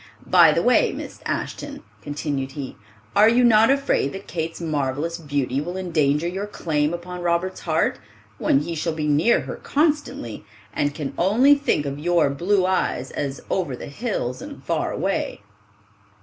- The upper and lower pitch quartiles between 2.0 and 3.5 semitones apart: No, average, 4.7 semitones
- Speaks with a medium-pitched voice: Yes, medium, 165 Hz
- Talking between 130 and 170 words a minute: Yes, average, 165 wpm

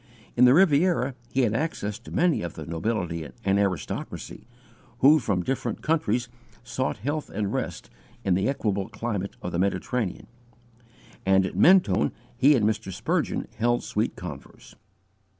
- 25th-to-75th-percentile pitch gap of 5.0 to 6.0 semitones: Yes, wide, 5.6 semitones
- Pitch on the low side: Yes, low, 110 Hz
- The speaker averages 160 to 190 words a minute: No, average, 150 wpm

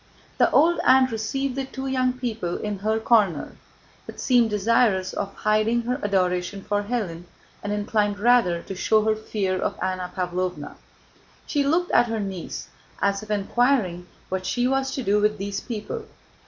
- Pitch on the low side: No, high, 210 Hz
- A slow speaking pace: No, average, 170 wpm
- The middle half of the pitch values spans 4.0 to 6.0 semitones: Yes, average, 4.3 semitones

